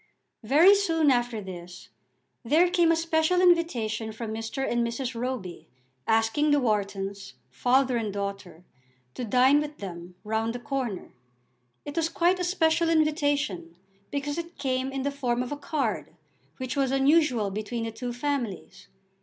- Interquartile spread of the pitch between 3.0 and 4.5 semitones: No, average, 5.3 semitones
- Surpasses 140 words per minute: Yes, average, 155 wpm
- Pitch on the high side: Yes, very high, 255 Hz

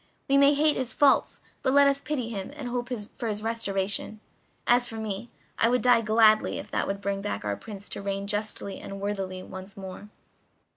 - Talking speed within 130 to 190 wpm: No, average, 200 wpm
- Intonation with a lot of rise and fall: No, average, 3.8 semitones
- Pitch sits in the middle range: No, high, 215 Hz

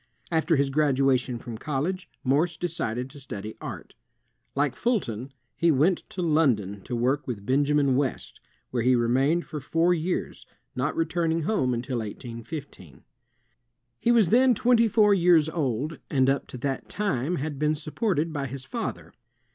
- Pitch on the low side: No, medium, 145 Hz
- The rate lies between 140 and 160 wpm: Yes, average, 155 wpm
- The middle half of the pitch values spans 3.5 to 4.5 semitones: No, average, 4.9 semitones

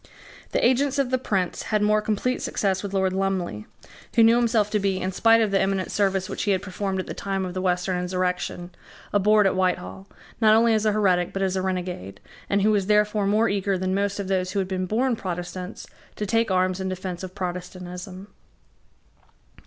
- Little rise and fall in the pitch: Yes, narrow, 2.3 semitones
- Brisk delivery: Yes, fast, 210 wpm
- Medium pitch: No, high, 195 Hz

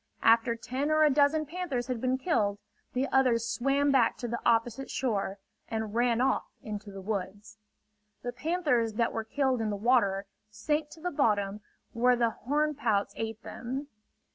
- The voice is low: No, high, 240 Hz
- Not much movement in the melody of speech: No, average, 3.8 semitones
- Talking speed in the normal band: Yes, average, 170 wpm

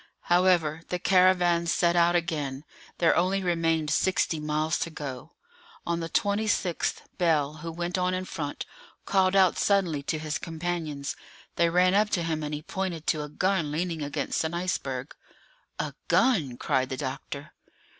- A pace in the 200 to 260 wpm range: No, average, 160 wpm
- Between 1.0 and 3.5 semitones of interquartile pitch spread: Yes, average, 3.1 semitones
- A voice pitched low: No, medium, 165 Hz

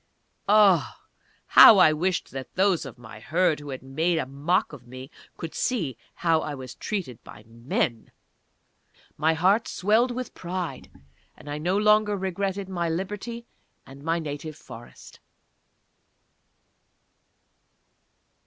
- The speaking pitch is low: No, medium, 165 Hz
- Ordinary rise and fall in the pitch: No, wide, 5.7 semitones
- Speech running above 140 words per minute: No, slow, 135 wpm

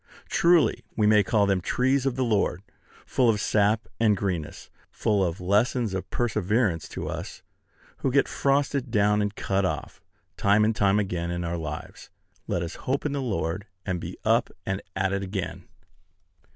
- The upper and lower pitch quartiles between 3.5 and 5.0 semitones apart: Yes, average, 4.2 semitones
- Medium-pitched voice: No, low, 105 Hz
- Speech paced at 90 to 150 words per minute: No, average, 175 wpm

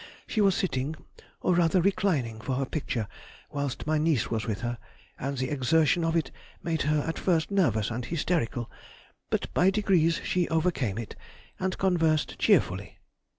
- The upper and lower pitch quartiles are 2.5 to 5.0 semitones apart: No, wide, 5.6 semitones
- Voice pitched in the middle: Yes, medium, 155 Hz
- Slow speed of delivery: No, average, 150 wpm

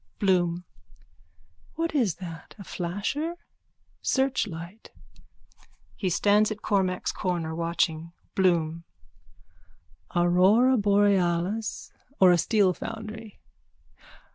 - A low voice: No, high, 190 Hz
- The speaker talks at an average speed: No, slow, 90 wpm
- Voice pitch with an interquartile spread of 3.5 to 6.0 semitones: Yes, average, 3.8 semitones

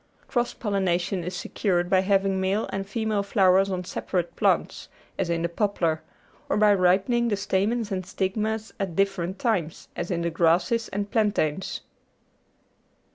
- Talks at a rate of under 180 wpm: Yes, average, 155 wpm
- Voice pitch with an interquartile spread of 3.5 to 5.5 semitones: No, narrow, 2.6 semitones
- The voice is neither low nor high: No, high, 195 Hz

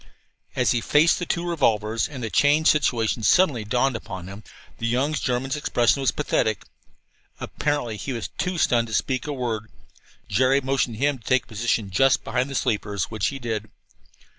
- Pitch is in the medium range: No, low, 125 Hz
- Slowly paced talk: No, average, 180 wpm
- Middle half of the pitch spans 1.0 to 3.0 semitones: No, average, 4.0 semitones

